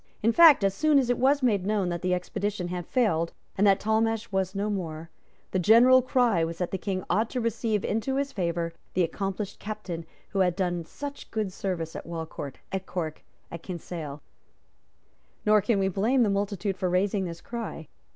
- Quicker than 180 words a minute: Yes, average, 190 wpm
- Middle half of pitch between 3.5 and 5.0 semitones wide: Yes, average, 4.0 semitones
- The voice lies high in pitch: Yes, high, 195 Hz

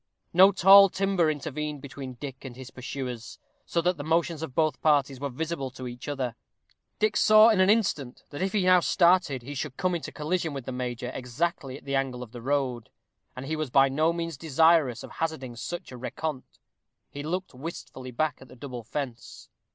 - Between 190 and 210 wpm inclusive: Yes, average, 200 wpm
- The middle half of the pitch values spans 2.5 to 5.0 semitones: Yes, average, 4.6 semitones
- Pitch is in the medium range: Yes, medium, 145 Hz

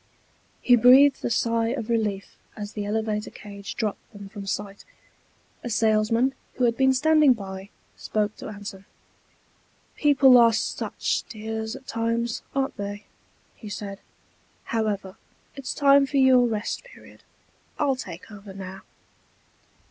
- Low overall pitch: No, high, 220 Hz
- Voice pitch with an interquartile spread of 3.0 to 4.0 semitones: Yes, average, 3.7 semitones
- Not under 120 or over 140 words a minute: Yes, slow, 135 wpm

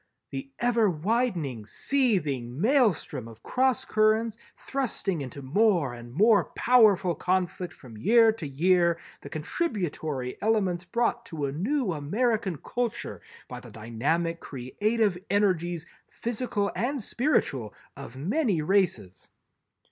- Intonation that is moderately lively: No, wide, 7.9 semitones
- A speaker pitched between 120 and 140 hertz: No, medium, 185 Hz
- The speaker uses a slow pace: Yes, slow, 115 wpm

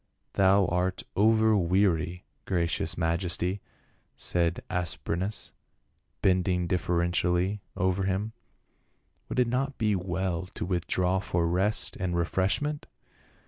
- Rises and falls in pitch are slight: Yes, narrow, 2.1 semitones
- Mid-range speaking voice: No, very low, 90 Hz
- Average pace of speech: No, slow, 105 wpm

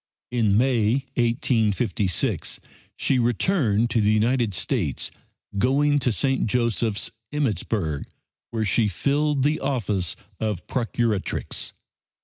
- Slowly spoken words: Yes, slow, 105 wpm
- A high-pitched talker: No, low, 115 Hz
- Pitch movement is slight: No, average, 4.0 semitones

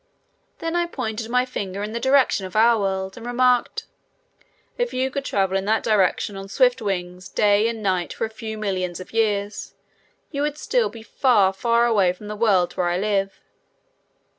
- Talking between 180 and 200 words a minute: Yes, average, 190 wpm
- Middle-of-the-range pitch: No, high, 215 Hz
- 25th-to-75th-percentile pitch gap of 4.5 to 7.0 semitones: No, average, 3.8 semitones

